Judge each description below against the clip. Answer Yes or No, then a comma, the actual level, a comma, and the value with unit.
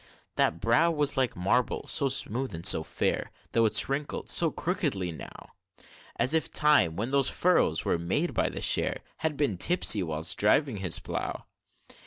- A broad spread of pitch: Yes, wide, 8.4 semitones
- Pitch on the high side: No, low, 125 Hz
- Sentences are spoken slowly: No, average, 170 wpm